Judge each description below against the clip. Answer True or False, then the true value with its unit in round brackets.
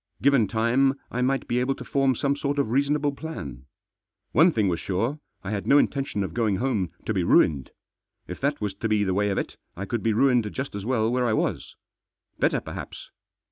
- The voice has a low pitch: True (120 Hz)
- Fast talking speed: True (215 wpm)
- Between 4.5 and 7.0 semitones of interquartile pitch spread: True (5.1 semitones)